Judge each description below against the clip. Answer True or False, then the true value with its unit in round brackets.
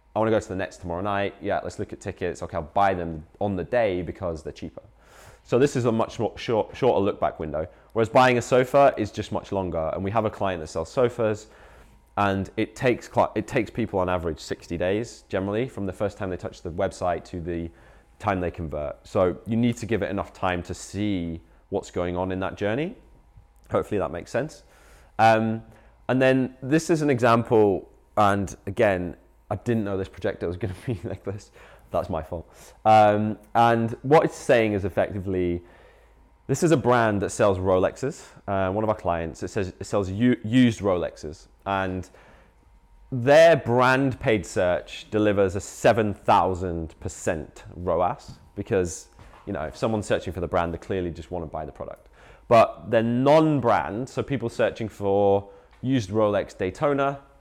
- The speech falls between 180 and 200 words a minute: True (190 wpm)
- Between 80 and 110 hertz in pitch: True (100 Hz)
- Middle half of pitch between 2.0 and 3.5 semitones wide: False (4.2 semitones)